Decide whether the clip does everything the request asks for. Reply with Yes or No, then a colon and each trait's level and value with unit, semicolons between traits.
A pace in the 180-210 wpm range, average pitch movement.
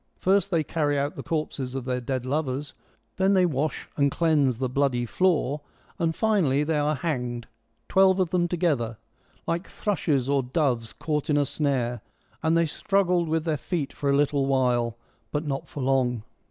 Yes: average, 190 wpm; average, 4.2 semitones